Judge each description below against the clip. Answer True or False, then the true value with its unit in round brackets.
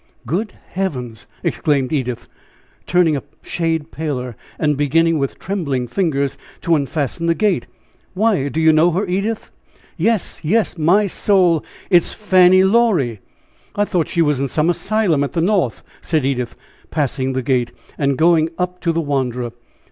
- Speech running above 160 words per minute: False (155 wpm)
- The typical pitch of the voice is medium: True (160 Hz)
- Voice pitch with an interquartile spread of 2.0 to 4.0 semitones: False (4.9 semitones)